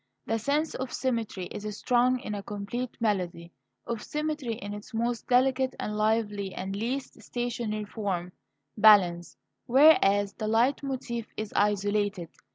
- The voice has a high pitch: Yes, high, 215 Hz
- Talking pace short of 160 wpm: Yes, average, 140 wpm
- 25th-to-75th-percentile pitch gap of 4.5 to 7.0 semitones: No, average, 3.4 semitones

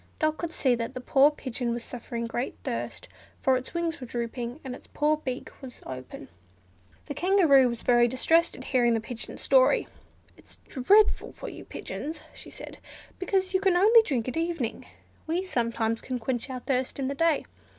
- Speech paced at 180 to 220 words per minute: Yes, average, 190 wpm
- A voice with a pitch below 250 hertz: No, very high, 265 Hz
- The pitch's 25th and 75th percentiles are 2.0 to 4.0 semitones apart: No, wide, 5.6 semitones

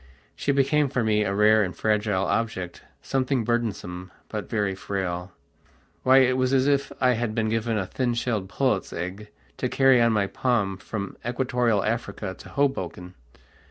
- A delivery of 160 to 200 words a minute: Yes, average, 165 wpm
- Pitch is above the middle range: No, low, 110 Hz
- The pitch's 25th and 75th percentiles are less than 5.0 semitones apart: Yes, average, 4.4 semitones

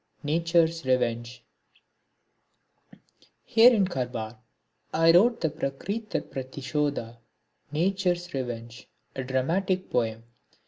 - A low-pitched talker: No, medium, 145 Hz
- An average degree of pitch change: No, wide, 6.1 semitones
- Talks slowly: Yes, slow, 90 wpm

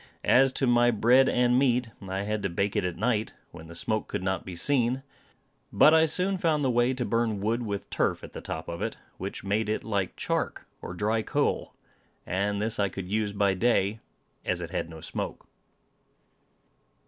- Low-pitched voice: Yes, low, 110 Hz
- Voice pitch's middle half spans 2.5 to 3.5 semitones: No, average, 3.9 semitones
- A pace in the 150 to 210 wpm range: Yes, average, 195 wpm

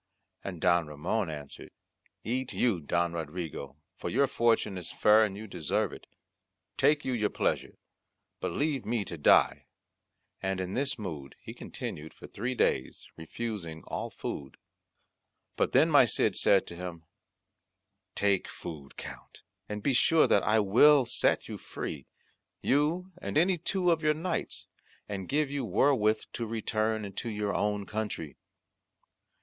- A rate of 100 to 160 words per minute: Yes, average, 150 wpm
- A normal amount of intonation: No, wide, 7.0 semitones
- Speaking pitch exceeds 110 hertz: No, low, 105 Hz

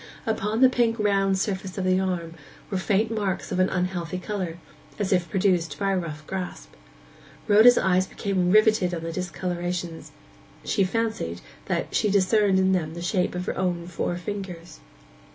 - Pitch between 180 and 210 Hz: Yes, medium, 185 Hz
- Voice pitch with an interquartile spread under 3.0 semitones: Yes, narrow, 2.4 semitones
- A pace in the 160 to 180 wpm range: Yes, average, 170 wpm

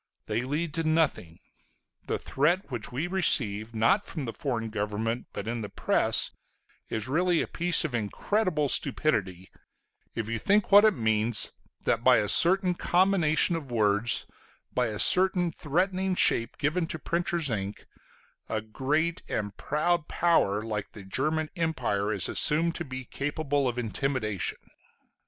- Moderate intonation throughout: No, wide, 7.4 semitones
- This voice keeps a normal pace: Yes, average, 150 wpm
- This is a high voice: No, medium, 140 Hz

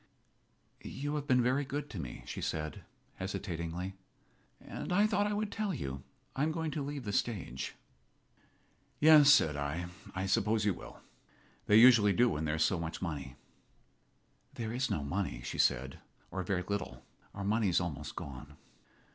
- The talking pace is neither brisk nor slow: Yes, average, 165 wpm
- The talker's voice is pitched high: No, low, 100 Hz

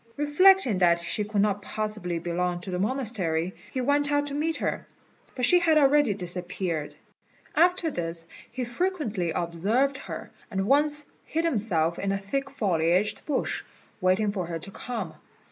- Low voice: No, high, 210 Hz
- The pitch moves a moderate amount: No, wide, 8.0 semitones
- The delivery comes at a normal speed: Yes, average, 160 wpm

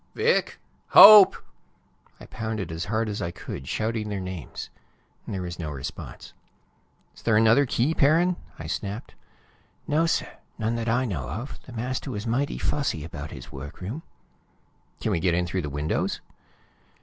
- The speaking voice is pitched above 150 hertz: No, low, 110 Hz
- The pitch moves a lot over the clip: Yes, wide, 6.8 semitones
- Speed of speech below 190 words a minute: Yes, average, 160 wpm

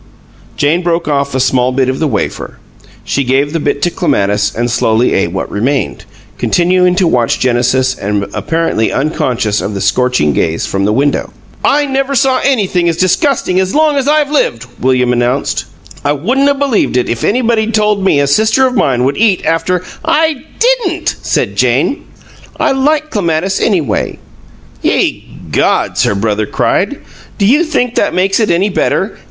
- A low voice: No, medium, 165 Hz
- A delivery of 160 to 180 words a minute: Yes, average, 175 wpm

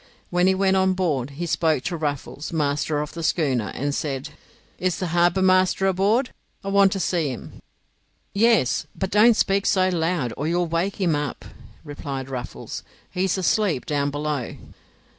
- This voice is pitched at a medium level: Yes, medium, 170 Hz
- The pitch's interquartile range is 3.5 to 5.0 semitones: Yes, average, 4.6 semitones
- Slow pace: No, average, 170 wpm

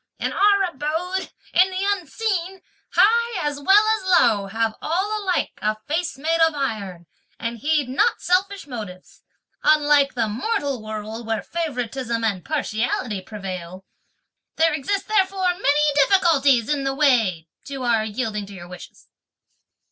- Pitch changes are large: Yes, wide, 8.3 semitones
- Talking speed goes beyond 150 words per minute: No, average, 140 wpm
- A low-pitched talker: No, very high, 280 Hz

